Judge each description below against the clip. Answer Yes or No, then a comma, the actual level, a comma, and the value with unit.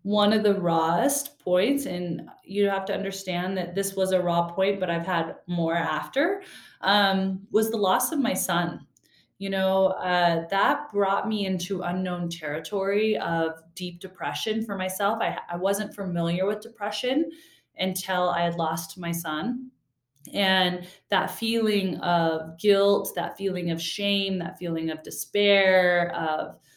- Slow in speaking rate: No, average, 150 wpm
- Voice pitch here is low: No, high, 190 Hz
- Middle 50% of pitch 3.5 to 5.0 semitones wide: No, average, 2.8 semitones